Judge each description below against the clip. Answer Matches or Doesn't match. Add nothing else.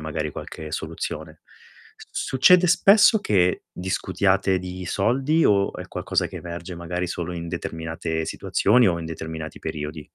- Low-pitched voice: Matches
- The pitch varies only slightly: Doesn't match